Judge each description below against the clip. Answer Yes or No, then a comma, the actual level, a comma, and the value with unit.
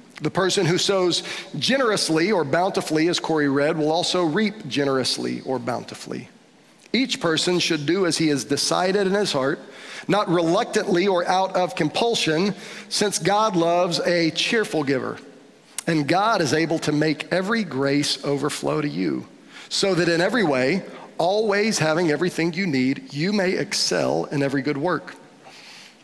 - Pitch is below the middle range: No, medium, 170 Hz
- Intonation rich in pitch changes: No, average, 4.5 semitones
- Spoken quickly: No, average, 155 wpm